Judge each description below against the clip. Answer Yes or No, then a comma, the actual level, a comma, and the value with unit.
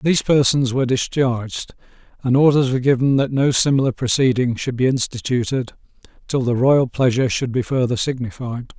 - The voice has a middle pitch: No, low, 130 Hz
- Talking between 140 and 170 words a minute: Yes, average, 155 wpm